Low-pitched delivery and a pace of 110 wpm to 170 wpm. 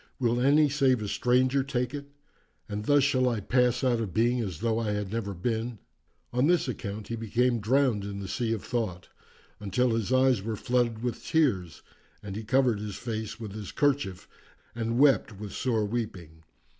No: low, 115 Hz; average, 185 wpm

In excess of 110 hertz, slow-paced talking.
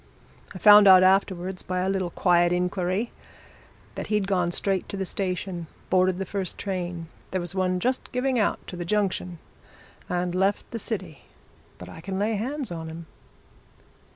No: medium, 185 Hz; average, 170 wpm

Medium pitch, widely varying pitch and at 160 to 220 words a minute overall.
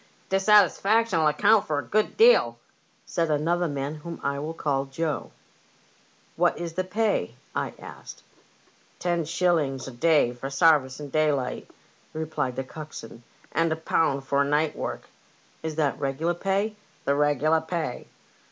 No: medium, 155 Hz; average, 3.6 semitones; average, 170 wpm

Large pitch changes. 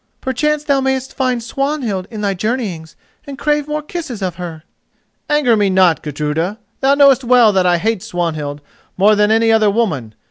Yes: wide, 6.8 semitones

